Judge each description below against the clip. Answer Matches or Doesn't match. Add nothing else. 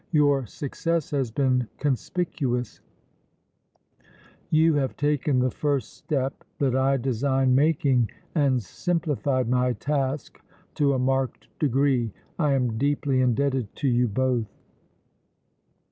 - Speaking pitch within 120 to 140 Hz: Matches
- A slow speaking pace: Matches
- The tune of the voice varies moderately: Doesn't match